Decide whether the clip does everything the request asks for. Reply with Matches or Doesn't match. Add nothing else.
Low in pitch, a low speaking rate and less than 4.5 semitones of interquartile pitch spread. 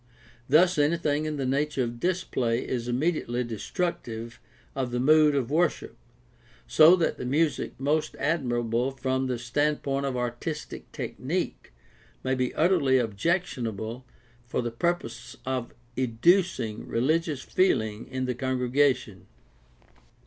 Matches